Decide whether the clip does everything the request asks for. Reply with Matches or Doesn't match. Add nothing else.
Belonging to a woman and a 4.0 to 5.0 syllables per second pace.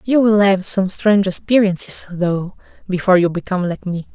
Doesn't match